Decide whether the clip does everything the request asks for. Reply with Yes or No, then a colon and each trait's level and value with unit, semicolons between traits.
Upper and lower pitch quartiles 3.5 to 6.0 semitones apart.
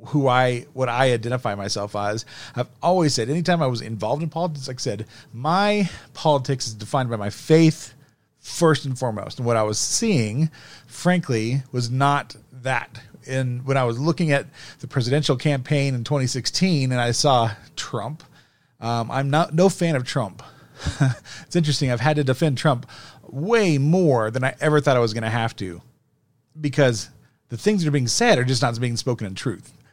Yes: average, 4.2 semitones